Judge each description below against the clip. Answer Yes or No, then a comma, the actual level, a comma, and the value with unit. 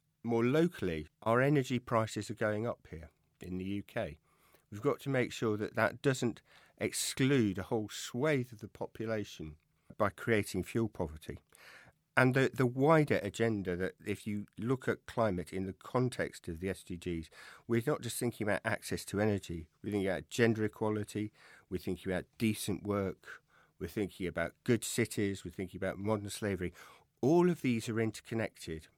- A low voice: Yes, low, 105 Hz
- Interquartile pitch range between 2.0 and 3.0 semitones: No, average, 4.1 semitones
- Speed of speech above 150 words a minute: Yes, average, 170 wpm